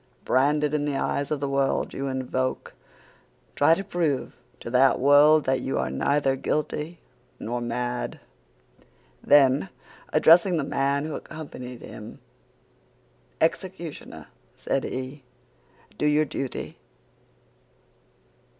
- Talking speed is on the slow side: Yes, slow, 115 wpm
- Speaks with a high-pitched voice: No, medium, 140 Hz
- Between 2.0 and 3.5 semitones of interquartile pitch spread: Yes, narrow, 2.6 semitones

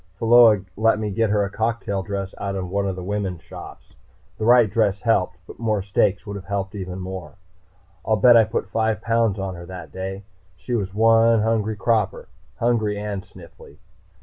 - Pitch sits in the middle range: No, low, 100 Hz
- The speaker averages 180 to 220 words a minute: Yes, average, 185 wpm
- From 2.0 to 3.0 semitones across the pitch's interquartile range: Yes, average, 2.7 semitones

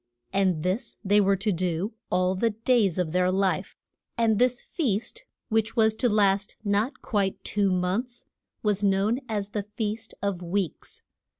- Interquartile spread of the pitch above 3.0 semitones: No, average, 2.7 semitones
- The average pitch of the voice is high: Yes, high, 205 Hz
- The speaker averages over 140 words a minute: Yes, average, 165 wpm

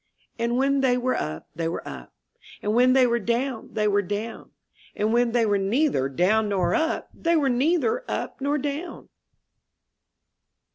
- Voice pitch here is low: No, high, 240 Hz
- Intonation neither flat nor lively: Yes, average, 4.9 semitones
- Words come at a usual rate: Yes, average, 170 wpm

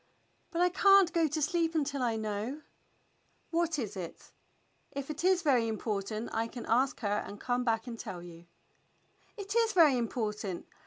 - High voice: Yes, very high, 250 Hz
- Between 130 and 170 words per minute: Yes, average, 150 wpm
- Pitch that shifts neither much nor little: No, wide, 6.7 semitones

